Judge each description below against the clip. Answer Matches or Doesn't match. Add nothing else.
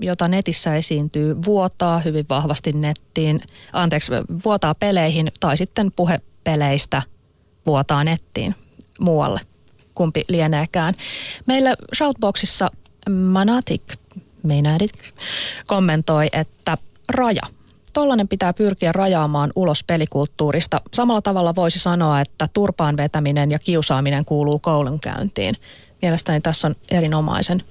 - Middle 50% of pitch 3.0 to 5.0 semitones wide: Matches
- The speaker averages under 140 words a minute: Matches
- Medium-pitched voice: Matches